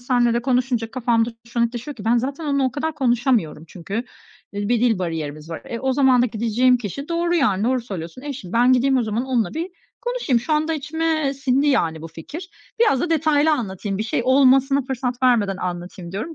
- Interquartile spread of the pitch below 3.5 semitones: No, average, 4.4 semitones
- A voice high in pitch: Yes, very high, 250 Hz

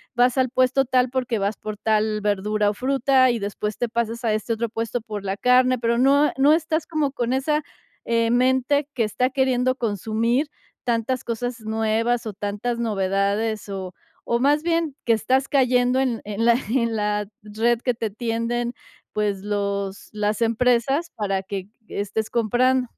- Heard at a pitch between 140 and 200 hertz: No, high, 235 Hz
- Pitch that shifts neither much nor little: Yes, average, 3.3 semitones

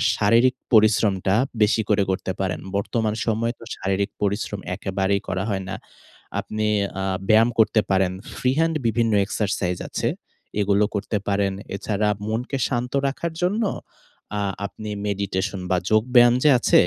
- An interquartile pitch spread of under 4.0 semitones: Yes, average, 2.8 semitones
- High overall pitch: No, low, 105 Hz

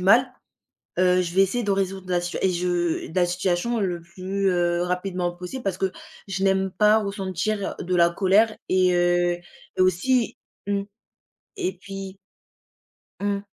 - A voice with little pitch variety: Yes, narrow, 2.0 semitones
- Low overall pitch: No, medium, 185 Hz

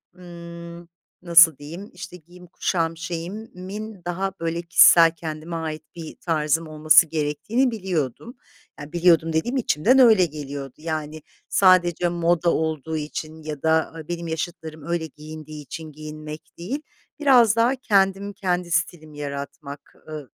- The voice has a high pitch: No, medium, 165 Hz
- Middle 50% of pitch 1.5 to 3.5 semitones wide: Yes, narrow, 2.6 semitones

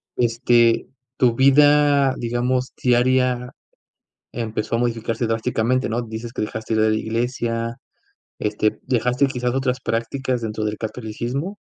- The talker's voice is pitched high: No, low, 120 Hz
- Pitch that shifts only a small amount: Yes, narrow, 2.1 semitones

